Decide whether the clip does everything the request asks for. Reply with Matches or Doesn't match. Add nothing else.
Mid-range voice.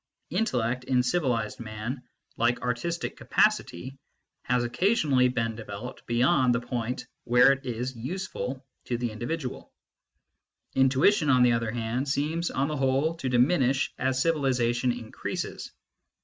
Doesn't match